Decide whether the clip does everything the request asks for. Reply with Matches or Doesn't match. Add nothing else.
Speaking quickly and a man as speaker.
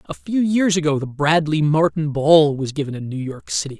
Matches